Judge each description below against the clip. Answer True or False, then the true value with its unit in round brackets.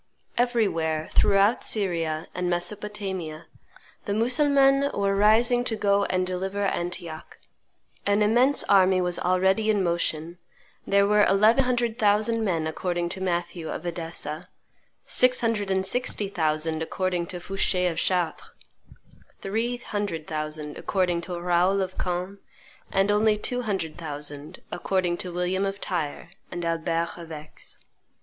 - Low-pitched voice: False (185 Hz)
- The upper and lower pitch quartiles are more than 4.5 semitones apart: False (3.4 semitones)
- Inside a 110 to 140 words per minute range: True (135 wpm)